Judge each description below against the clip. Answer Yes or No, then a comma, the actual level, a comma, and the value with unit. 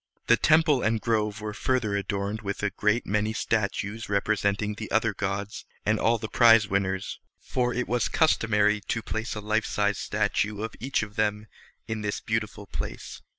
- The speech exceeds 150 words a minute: Yes, average, 175 wpm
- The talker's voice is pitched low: Yes, low, 105 Hz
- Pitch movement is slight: Yes, narrow, 1.6 semitones